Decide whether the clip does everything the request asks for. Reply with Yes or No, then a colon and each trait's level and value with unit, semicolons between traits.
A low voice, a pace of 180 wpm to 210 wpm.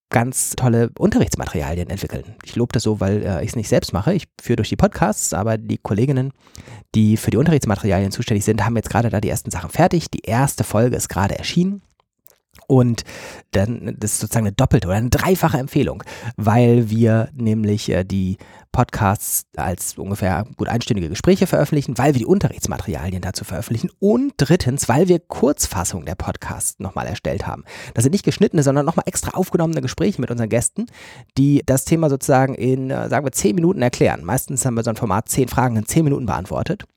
Yes: low, 120 Hz; average, 185 wpm